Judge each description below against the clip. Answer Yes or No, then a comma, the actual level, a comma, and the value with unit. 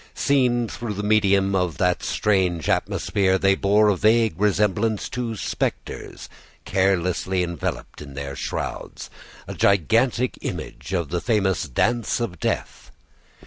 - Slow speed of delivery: Yes, slow, 130 wpm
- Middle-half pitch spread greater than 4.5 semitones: No, average, 3.4 semitones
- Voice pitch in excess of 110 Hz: No, low, 100 Hz